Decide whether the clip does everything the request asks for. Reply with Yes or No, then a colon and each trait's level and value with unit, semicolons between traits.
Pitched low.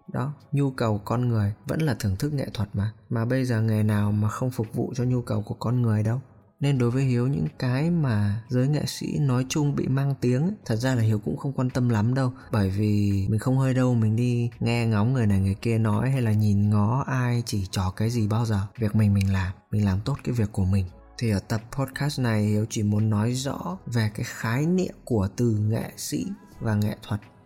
Yes: low, 115 Hz